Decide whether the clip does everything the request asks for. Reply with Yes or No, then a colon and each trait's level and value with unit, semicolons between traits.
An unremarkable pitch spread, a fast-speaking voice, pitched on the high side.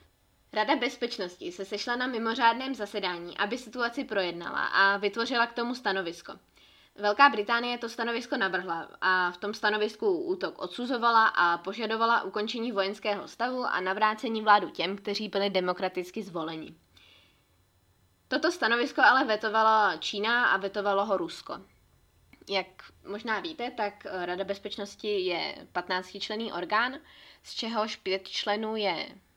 No: average, 3.6 semitones; average, 130 wpm; high, 210 Hz